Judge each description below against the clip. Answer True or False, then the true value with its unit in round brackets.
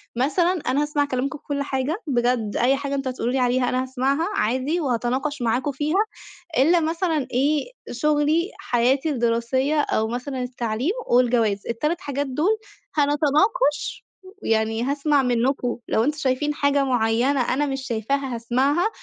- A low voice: False (270 Hz)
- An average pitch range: True (3.2 semitones)